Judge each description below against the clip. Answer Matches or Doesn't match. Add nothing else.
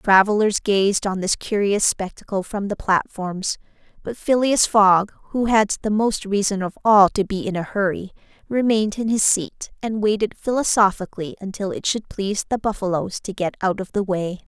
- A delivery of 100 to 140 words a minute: Doesn't match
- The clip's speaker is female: Matches